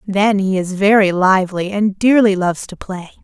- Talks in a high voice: Yes, high, 195 Hz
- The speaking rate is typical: Yes, average, 185 wpm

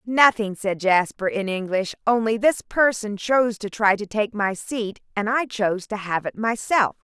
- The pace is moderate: Yes, average, 185 wpm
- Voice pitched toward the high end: Yes, high, 215 Hz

